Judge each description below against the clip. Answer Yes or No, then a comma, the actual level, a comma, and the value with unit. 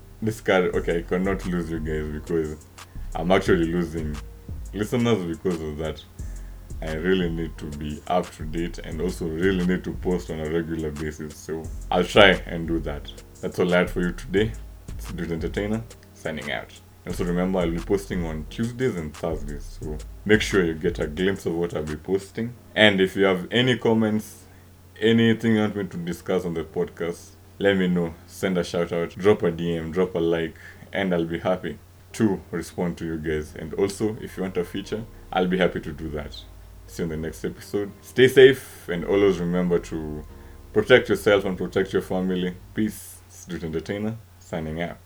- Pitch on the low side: Yes, very low, 90 Hz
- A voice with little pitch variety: No, average, 3.0 semitones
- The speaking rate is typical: Yes, average, 195 wpm